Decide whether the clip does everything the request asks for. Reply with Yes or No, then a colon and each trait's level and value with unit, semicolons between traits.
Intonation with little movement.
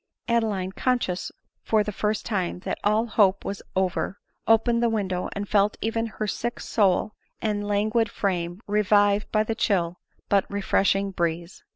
Yes: narrow, 2.3 semitones